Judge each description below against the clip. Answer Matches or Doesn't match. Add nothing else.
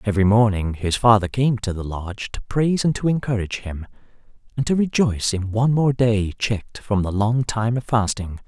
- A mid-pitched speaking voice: Doesn't match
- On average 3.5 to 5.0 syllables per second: Doesn't match